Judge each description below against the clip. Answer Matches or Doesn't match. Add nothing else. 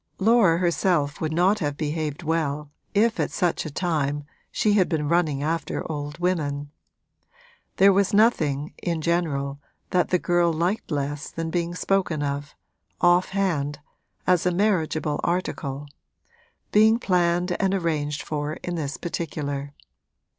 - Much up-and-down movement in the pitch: Doesn't match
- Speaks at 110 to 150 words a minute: Matches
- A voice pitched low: Doesn't match